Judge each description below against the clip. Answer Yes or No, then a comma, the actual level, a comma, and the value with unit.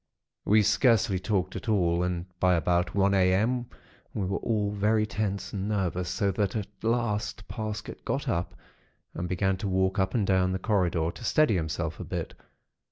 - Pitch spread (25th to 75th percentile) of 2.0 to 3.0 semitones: Yes, narrow, 2.6 semitones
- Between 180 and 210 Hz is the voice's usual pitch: No, very low, 95 Hz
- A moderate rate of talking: Yes, average, 175 wpm